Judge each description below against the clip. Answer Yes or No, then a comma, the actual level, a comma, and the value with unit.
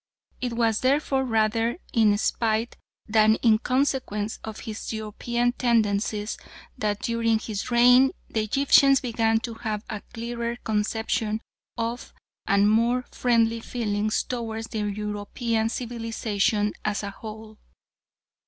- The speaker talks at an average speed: No, slow, 115 wpm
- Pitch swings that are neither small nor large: No, narrow, 1.9 semitones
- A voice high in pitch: Yes, high, 225 Hz